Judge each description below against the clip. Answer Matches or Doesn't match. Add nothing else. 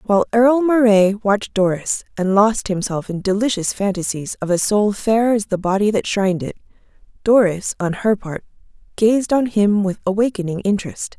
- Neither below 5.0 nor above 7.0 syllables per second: Matches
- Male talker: Doesn't match